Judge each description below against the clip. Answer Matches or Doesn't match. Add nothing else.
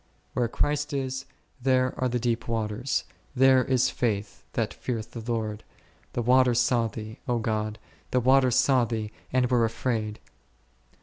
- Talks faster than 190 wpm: Doesn't match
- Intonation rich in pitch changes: Doesn't match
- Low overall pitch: Matches